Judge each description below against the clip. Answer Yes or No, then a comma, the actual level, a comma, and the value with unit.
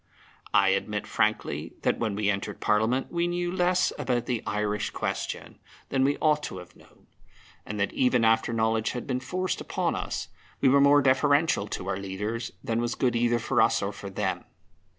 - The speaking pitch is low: Yes, low, 120 Hz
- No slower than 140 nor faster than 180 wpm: No, average, 190 wpm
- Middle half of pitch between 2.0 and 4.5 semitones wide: No, average, 4.9 semitones